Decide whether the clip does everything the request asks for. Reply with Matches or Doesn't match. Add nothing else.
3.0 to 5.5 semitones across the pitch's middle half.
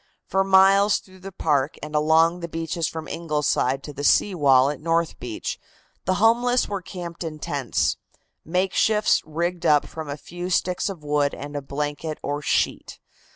Matches